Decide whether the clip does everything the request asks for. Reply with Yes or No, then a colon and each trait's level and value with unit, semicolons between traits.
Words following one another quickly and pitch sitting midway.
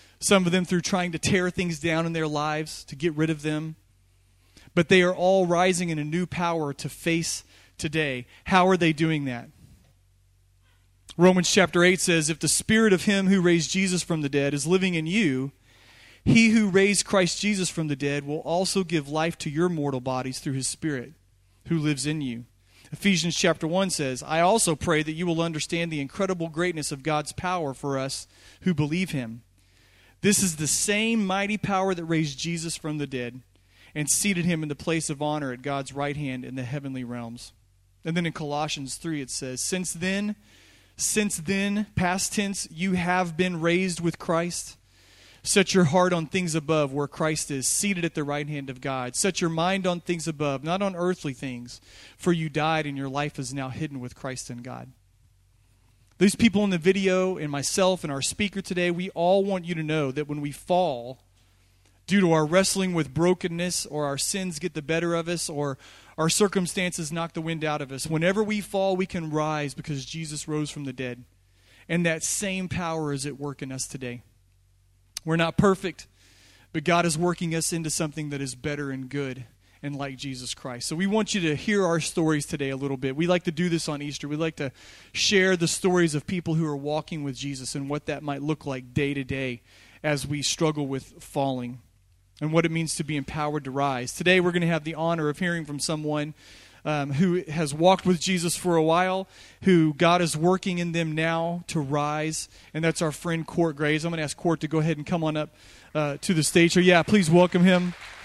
Yes: fast, 210 wpm; medium, 155 Hz